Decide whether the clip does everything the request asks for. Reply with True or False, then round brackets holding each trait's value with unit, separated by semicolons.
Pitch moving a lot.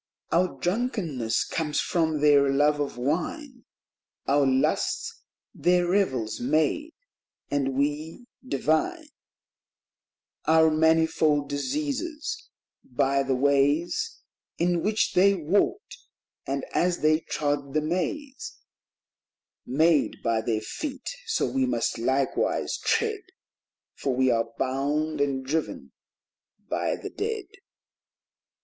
True (6.6 semitones)